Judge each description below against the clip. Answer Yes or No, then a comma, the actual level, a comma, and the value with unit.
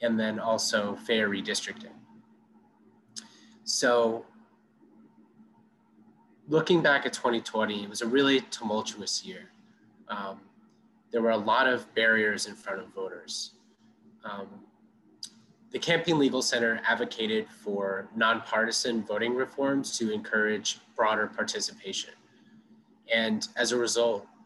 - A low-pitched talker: Yes, low, 130 Hz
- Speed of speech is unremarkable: No, slow, 110 wpm